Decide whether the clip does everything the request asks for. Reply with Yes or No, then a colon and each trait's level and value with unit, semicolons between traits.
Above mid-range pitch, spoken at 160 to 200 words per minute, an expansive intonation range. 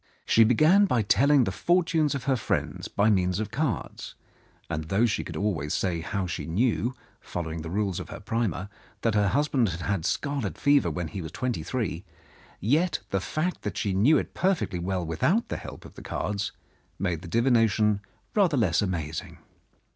No: low, 105 Hz; average, 185 wpm; wide, 6.7 semitones